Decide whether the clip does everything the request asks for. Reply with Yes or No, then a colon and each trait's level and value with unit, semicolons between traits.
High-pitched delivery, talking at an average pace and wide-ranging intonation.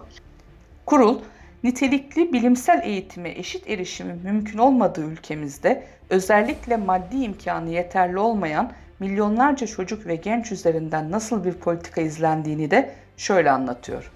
Yes: high, 210 Hz; average, 110 wpm; wide, 6.2 semitones